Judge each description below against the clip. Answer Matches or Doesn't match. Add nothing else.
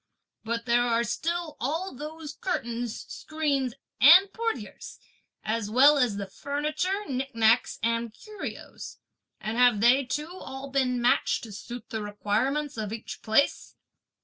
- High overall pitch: Matches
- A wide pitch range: Doesn't match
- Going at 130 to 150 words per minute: Matches